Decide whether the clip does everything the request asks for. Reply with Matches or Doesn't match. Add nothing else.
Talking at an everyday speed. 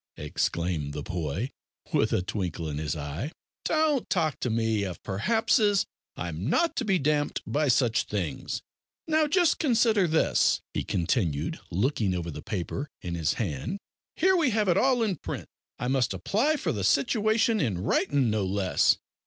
Matches